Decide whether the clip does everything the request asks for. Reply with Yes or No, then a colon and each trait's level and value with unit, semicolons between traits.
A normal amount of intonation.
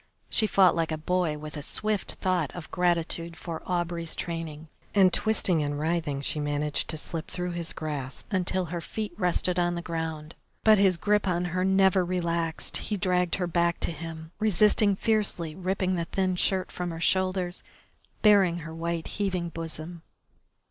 No: narrow, 2.3 semitones